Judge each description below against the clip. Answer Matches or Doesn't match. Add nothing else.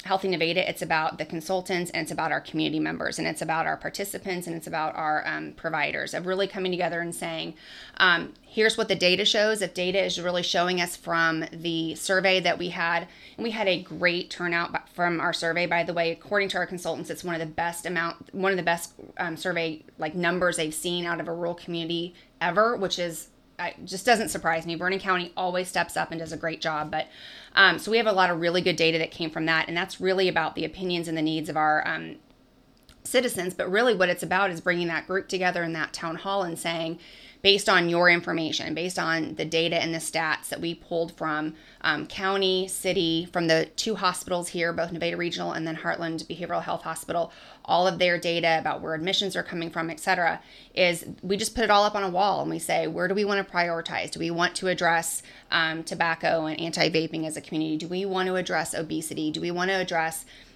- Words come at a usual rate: Doesn't match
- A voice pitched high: Doesn't match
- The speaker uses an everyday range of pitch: Doesn't match